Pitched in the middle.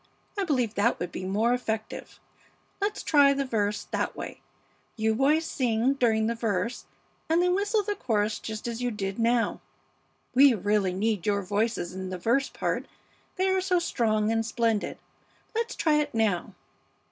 No: high, 230 Hz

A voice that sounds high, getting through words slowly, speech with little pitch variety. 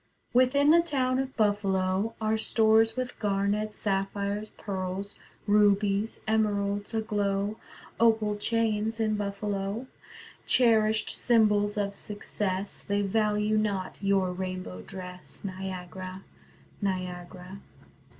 Yes: high, 205 Hz; slow, 100 wpm; narrow, 2.1 semitones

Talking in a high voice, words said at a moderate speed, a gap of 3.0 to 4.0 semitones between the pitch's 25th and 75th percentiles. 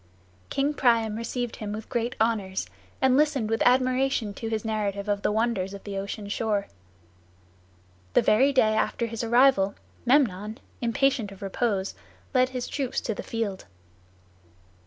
Yes: high, 225 Hz; average, 150 wpm; average, 3.5 semitones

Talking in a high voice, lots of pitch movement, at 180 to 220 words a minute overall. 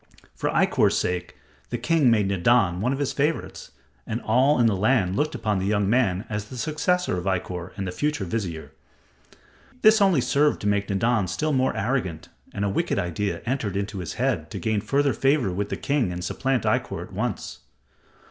No: low, 110 Hz; wide, 5.8 semitones; average, 190 wpm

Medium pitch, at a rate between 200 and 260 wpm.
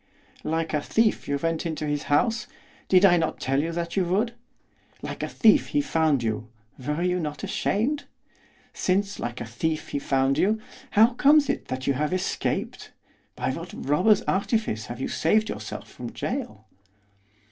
No: medium, 170 Hz; average, 170 wpm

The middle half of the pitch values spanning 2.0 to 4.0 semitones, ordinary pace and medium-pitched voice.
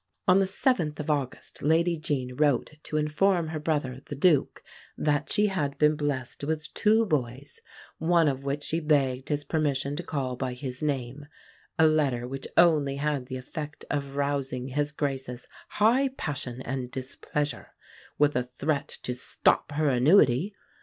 Yes: average, 2.9 semitones; average, 160 wpm; medium, 145 Hz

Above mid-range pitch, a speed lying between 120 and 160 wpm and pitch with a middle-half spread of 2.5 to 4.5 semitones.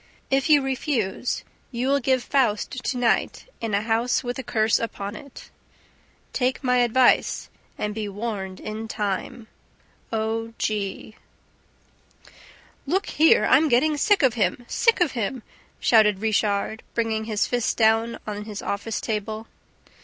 Yes: high, 225 Hz; average, 140 wpm; average, 3.2 semitones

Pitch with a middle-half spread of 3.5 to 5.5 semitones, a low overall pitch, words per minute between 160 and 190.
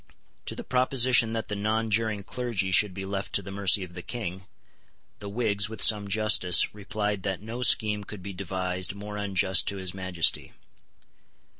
No: narrow, 2.4 semitones; low, 100 Hz; average, 170 wpm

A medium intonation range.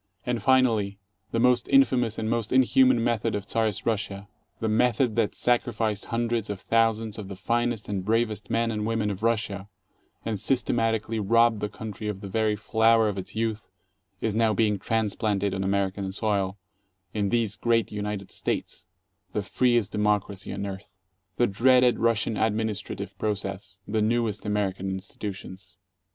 No: narrow, 2.3 semitones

